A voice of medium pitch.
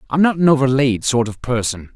No: low, 130 Hz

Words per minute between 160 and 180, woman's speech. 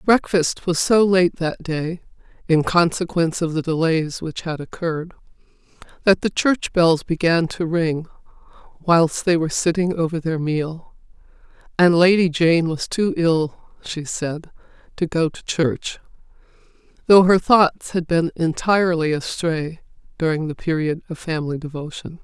No: average, 145 wpm; female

